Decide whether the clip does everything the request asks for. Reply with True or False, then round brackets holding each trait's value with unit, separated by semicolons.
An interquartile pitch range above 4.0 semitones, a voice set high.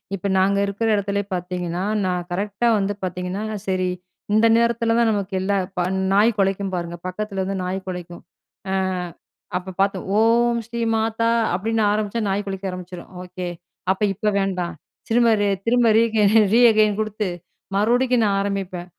False (3.3 semitones; 200 Hz)